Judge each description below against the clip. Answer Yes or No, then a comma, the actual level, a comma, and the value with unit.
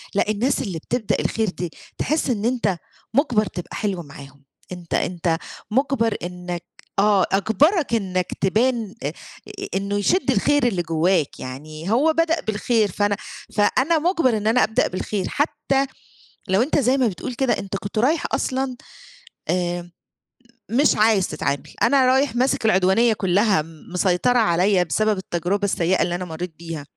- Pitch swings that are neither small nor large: No, wide, 5.7 semitones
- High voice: Yes, high, 205 Hz